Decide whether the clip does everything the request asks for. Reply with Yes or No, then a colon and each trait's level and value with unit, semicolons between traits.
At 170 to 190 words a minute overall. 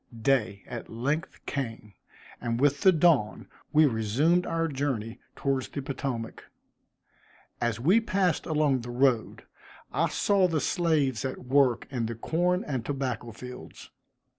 No: average, 140 wpm